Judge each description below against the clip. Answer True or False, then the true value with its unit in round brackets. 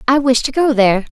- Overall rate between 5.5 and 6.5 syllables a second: True (6.3 syllables/s)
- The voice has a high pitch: True (255 Hz)